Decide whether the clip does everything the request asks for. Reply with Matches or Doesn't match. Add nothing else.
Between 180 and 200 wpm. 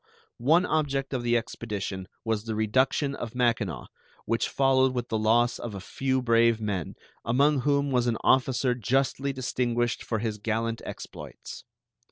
Doesn't match